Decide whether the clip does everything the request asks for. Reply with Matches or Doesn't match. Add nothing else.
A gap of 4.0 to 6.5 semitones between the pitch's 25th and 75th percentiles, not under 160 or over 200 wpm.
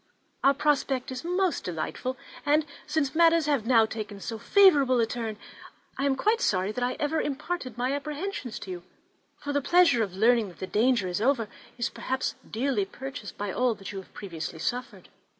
Matches